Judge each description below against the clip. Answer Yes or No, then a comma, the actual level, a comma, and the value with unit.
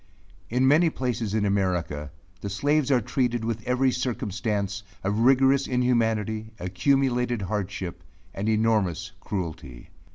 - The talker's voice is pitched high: No, low, 110 Hz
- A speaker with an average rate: No, slow, 120 wpm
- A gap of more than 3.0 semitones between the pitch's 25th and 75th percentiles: Yes, average, 4.0 semitones